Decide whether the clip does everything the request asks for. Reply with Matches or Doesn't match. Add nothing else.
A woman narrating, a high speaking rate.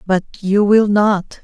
Doesn't match